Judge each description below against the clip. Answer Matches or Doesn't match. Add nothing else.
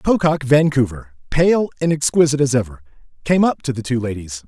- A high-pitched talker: Doesn't match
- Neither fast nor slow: Matches